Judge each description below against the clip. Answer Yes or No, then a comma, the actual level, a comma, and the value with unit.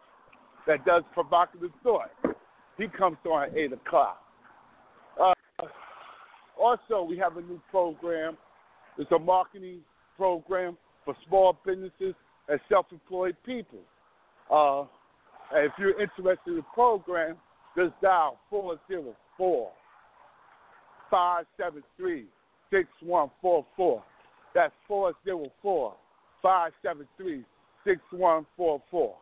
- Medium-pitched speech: Yes, medium, 180 Hz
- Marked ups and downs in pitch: No, average, 3.0 semitones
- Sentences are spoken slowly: Yes, slow, 90 wpm